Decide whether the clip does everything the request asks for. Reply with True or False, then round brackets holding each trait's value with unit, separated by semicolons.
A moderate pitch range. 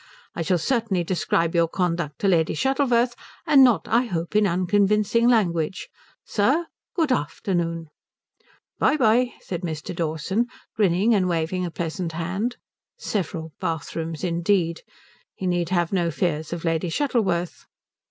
True (4.3 semitones)